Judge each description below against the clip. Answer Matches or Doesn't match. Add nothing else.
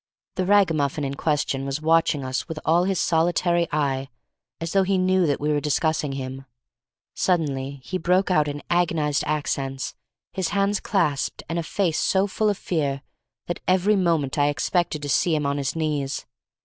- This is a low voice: Doesn't match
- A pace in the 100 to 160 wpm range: Doesn't match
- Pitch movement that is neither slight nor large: Matches